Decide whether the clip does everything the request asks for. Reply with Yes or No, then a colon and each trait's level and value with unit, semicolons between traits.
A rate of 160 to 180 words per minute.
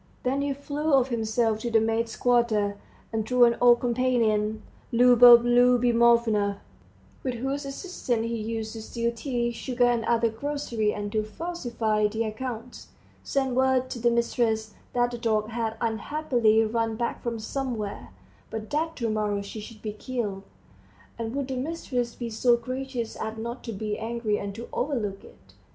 Yes: average, 165 wpm